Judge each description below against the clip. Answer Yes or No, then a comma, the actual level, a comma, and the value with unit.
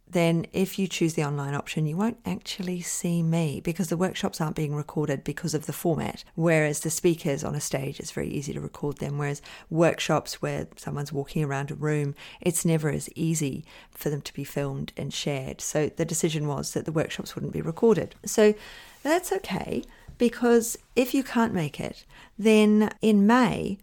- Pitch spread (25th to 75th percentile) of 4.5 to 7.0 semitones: Yes, wide, 5.4 semitones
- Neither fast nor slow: Yes, average, 190 wpm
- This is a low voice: No, medium, 165 Hz